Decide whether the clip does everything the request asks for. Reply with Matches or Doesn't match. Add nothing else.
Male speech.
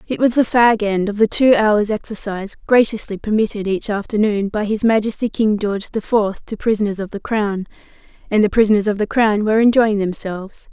Doesn't match